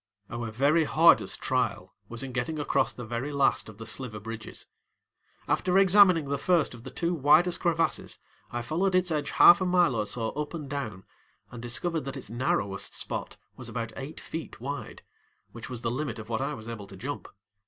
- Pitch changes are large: Yes, wide, 5.7 semitones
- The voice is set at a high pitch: No, low, 135 Hz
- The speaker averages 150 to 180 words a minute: No, average, 195 wpm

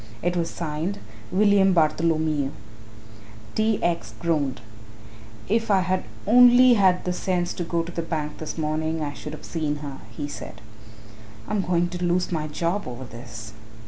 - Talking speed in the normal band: Yes, average, 160 wpm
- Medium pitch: Yes, medium, 170 Hz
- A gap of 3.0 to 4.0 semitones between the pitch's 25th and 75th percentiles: Yes, average, 3.4 semitones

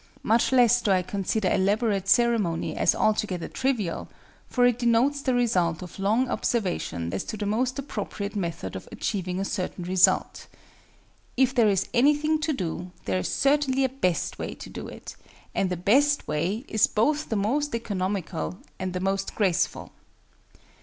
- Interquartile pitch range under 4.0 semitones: No, average, 5.1 semitones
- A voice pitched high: Yes, high, 210 Hz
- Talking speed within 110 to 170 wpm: Yes, average, 165 wpm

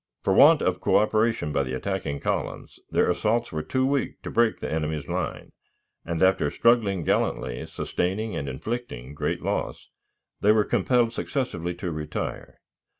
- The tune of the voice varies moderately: No, wide, 7.2 semitones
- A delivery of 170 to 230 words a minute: No, average, 150 wpm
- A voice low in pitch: Yes, very low, 95 Hz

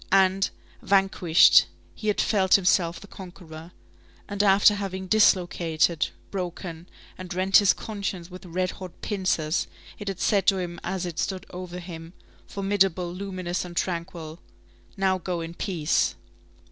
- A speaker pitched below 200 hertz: Yes, medium, 185 Hz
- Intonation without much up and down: Yes, narrow, 2.1 semitones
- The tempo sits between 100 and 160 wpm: Yes, average, 140 wpm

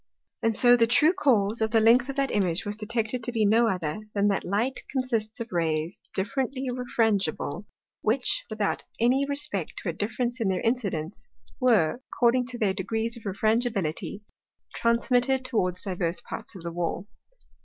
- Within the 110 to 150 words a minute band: No, average, 165 wpm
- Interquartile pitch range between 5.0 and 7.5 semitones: No, average, 4.0 semitones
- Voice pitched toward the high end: Yes, high, 225 Hz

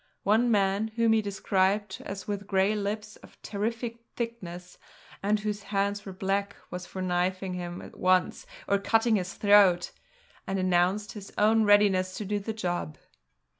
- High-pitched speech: Yes, high, 200 Hz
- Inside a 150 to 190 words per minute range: Yes, average, 160 wpm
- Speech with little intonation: Yes, narrow, 2.2 semitones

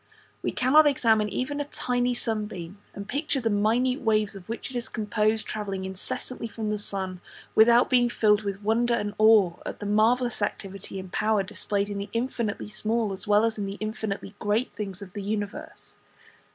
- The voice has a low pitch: No, high, 215 Hz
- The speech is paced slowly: No, average, 185 wpm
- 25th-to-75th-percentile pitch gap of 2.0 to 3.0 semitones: Yes, narrow, 2.6 semitones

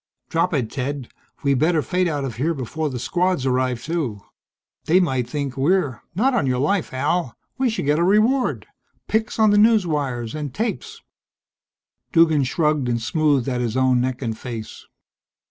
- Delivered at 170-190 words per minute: Yes, average, 175 wpm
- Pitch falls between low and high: Yes, medium, 145 Hz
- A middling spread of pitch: No, wide, 5.8 semitones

